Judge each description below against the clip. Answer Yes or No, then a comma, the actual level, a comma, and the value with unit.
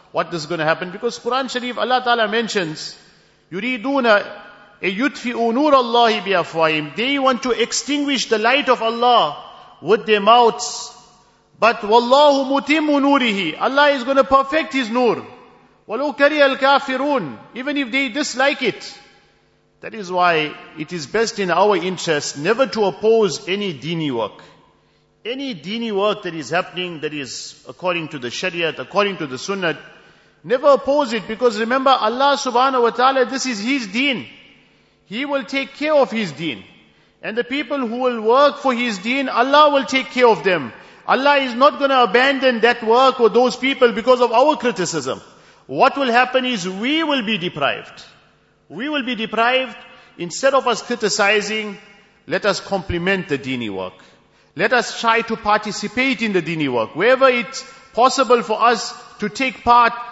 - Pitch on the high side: Yes, high, 235 Hz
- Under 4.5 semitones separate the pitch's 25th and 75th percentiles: No, average, 5.0 semitones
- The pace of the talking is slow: No, average, 160 wpm